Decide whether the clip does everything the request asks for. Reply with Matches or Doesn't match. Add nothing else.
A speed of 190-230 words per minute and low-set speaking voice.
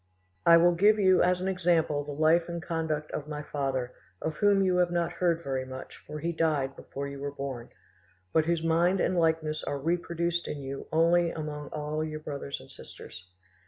Doesn't match